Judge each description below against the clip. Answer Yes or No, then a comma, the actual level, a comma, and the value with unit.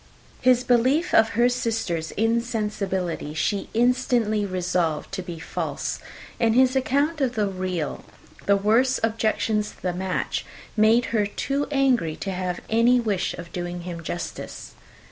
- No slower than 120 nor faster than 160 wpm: Yes, average, 145 wpm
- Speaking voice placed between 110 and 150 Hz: No, high, 215 Hz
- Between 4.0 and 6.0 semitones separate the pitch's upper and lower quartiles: Yes, average, 5.1 semitones